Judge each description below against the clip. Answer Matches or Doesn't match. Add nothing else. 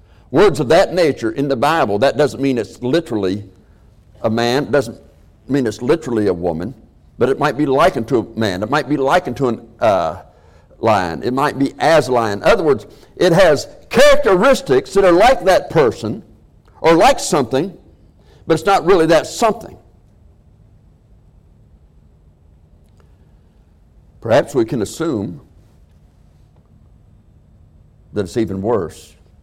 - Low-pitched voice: Matches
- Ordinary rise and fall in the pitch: Doesn't match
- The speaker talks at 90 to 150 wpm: Matches